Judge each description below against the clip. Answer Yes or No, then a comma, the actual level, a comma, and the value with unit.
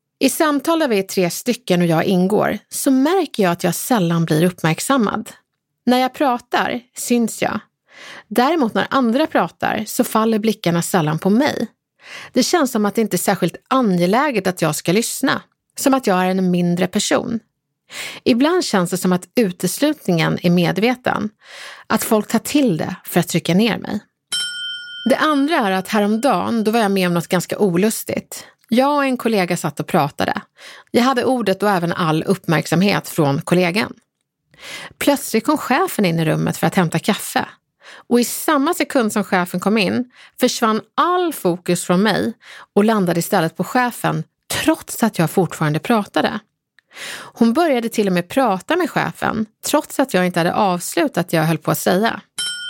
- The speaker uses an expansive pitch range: Yes, wide, 6.3 semitones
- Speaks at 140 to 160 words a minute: No, average, 175 wpm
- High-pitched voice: Yes, high, 210 Hz